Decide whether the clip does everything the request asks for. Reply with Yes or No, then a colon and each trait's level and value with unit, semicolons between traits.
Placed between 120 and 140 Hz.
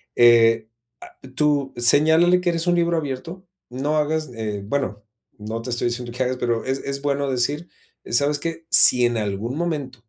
Yes: low, 135 Hz